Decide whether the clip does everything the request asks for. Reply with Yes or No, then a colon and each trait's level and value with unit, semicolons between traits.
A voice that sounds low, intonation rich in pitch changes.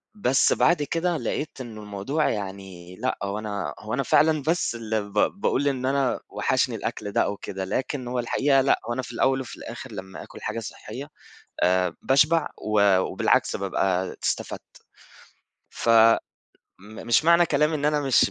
Yes: low, 120 Hz; wide, 5.8 semitones